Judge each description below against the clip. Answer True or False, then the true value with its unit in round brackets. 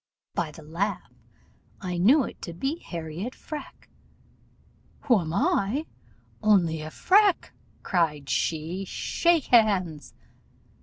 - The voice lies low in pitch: False (185 Hz)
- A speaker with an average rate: False (110 wpm)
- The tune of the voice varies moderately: False (7.2 semitones)